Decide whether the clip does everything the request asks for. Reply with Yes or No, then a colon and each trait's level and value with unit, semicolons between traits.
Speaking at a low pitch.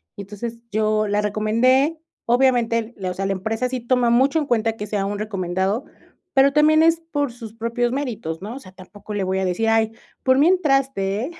No: high, 225 Hz